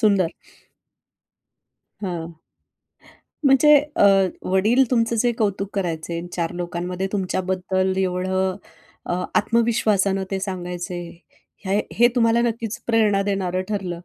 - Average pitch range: Yes, average, 3.3 semitones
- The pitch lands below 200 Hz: Yes, high, 190 Hz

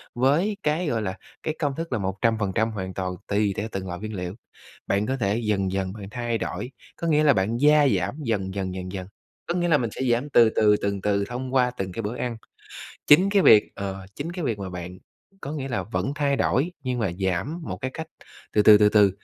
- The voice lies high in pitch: No, low, 110 Hz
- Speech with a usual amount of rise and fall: No, wide, 6.1 semitones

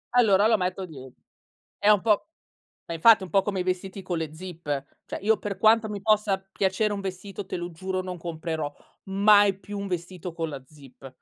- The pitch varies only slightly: No, average, 3.1 semitones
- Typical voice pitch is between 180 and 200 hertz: Yes, high, 190 Hz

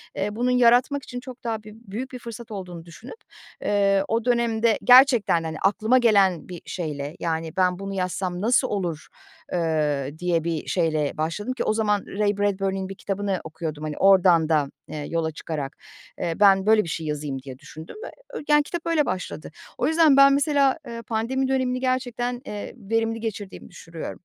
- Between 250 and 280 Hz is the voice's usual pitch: No, high, 200 Hz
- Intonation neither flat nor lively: No, wide, 6.3 semitones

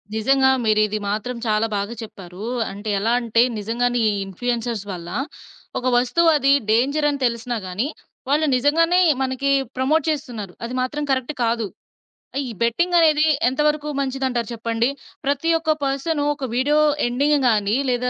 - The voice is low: No, very high, 250 Hz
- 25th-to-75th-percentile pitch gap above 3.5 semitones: Yes, average, 4.2 semitones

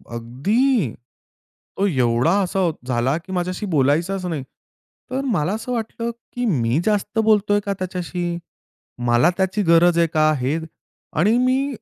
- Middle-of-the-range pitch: Yes, medium, 180 Hz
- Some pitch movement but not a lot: No, wide, 5.8 semitones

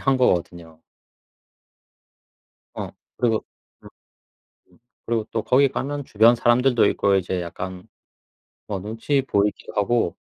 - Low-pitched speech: Yes, low, 110 Hz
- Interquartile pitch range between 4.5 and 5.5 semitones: Yes, average, 5.1 semitones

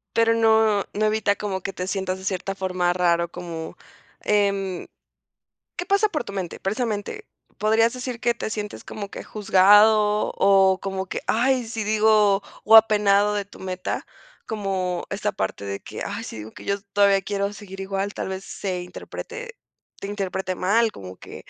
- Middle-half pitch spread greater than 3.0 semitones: No, narrow, 2.4 semitones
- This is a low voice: No, high, 200 Hz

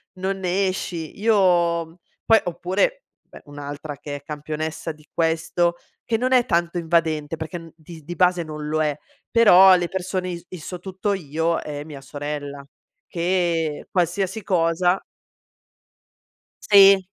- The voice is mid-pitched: Yes, medium, 170 Hz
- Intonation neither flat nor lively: Yes, average, 3.3 semitones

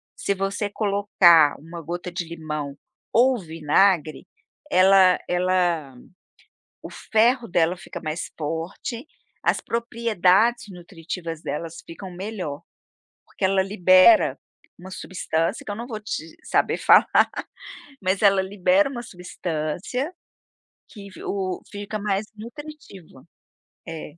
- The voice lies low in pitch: No, medium, 185 Hz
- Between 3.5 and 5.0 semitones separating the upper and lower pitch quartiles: Yes, average, 4.0 semitones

